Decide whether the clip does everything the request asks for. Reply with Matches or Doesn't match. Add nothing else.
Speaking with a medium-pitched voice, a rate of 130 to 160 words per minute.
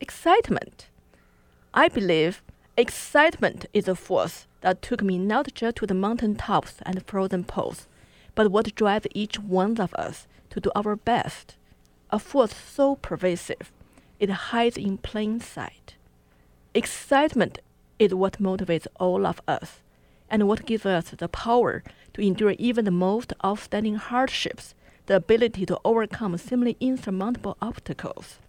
Doesn't match